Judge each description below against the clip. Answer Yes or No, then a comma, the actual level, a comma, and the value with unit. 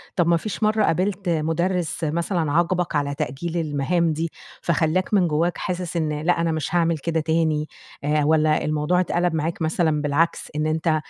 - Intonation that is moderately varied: No, narrow, 2.1 semitones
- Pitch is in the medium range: Yes, medium, 165 Hz